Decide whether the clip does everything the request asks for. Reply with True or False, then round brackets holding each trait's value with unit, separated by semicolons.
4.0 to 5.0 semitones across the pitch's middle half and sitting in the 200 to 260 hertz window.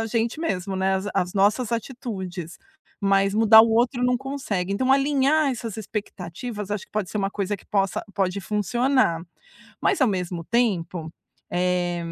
True (4.5 semitones; 205 Hz)